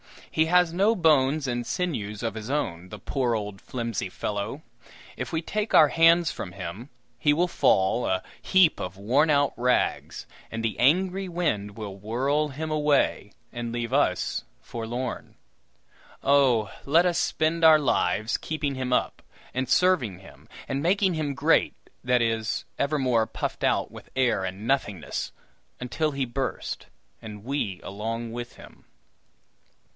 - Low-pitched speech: Yes, low, 130 Hz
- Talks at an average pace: Yes, average, 150 wpm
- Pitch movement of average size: No, wide, 5.9 semitones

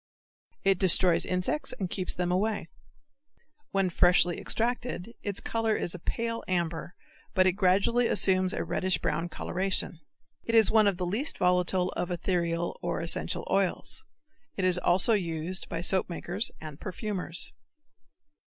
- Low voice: No, medium, 185 Hz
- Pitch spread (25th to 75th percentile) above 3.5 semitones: No, narrow, 2.5 semitones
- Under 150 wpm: Yes, average, 140 wpm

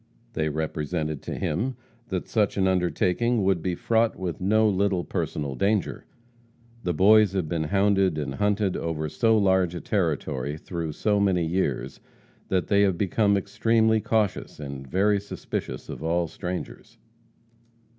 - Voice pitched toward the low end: Yes, very low, 95 Hz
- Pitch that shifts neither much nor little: Yes, average, 4.1 semitones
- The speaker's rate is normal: Yes, average, 145 wpm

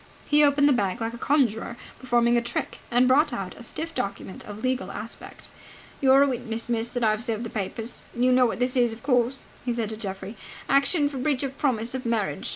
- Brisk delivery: Yes, fast, 220 wpm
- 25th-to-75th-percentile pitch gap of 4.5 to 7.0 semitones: No, average, 2.8 semitones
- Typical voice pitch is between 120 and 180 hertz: No, high, 240 Hz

